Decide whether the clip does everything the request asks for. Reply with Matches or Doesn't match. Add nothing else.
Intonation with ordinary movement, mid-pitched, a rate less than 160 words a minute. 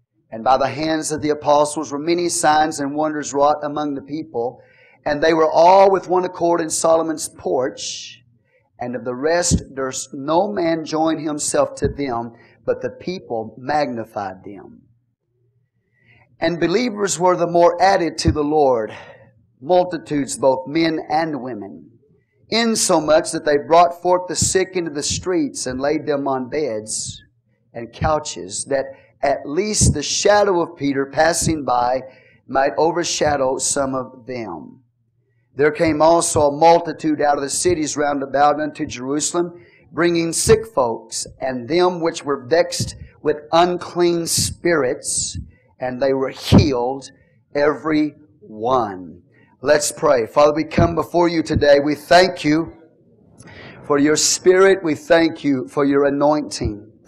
Matches